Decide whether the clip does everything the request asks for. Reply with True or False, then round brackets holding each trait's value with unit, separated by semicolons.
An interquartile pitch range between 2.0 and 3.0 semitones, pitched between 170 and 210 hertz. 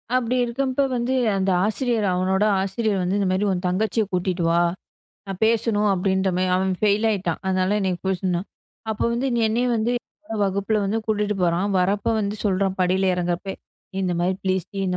True (2.7 semitones; 195 Hz)